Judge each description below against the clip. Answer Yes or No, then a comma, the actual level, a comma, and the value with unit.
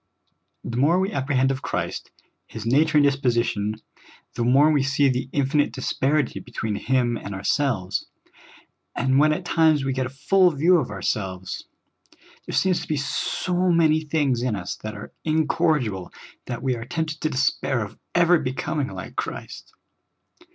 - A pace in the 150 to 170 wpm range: Yes, average, 165 wpm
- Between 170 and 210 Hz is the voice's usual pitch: No, low, 135 Hz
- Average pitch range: Yes, average, 4.5 semitones